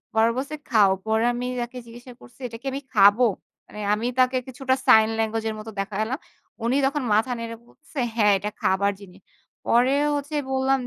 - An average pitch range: Yes, average, 3.3 semitones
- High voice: Yes, high, 230 Hz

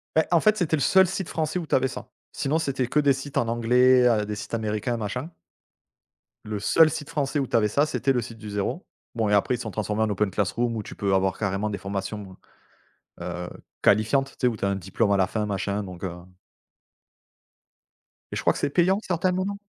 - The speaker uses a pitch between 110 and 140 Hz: Yes, low, 115 Hz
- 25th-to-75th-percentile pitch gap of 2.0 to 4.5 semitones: No, wide, 5.6 semitones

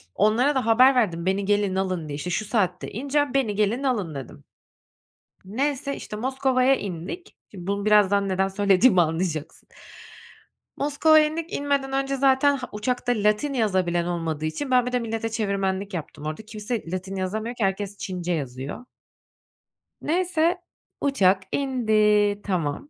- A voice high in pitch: Yes, high, 210 Hz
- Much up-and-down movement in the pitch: Yes, wide, 5.8 semitones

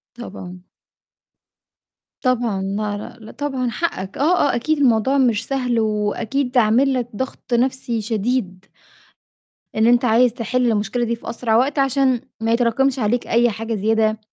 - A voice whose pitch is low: No, high, 235 Hz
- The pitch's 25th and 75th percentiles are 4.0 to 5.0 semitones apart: No, average, 2.9 semitones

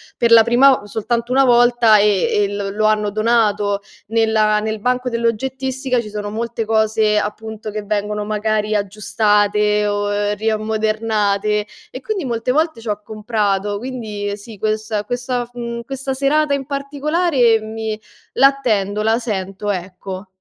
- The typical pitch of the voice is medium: No, high, 220 Hz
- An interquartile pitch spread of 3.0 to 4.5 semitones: No, narrow, 2.5 semitones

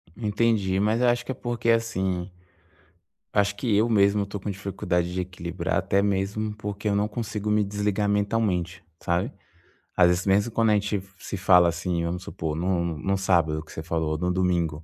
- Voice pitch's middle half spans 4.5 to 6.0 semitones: No, average, 2.9 semitones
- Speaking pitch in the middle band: No, very low, 95 Hz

